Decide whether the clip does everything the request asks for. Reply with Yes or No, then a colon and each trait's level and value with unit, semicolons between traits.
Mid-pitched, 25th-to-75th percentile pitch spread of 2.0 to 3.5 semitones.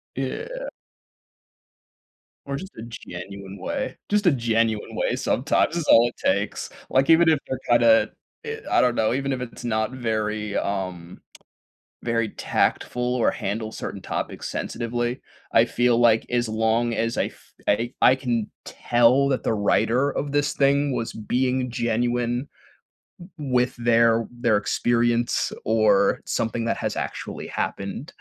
No: low, 120 Hz; average, 2.7 semitones